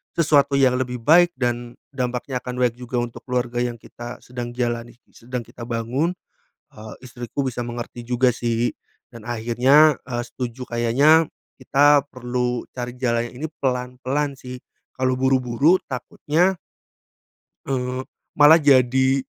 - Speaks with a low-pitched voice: Yes, low, 125 Hz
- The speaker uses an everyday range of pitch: No, narrow, 2.0 semitones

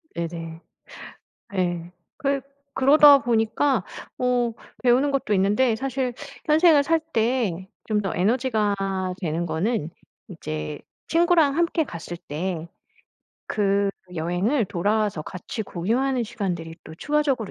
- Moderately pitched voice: No, high, 220 Hz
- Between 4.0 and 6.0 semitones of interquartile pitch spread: No, wide, 7.3 semitones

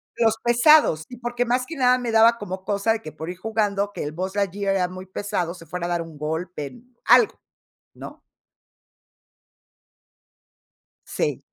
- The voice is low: No, high, 200 Hz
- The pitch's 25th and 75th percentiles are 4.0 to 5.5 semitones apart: Yes, average, 5.0 semitones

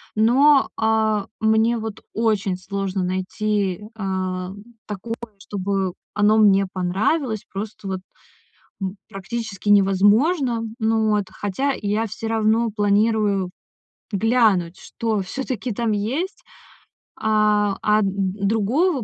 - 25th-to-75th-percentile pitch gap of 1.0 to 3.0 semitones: Yes, narrow, 2.4 semitones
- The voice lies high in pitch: Yes, high, 210 Hz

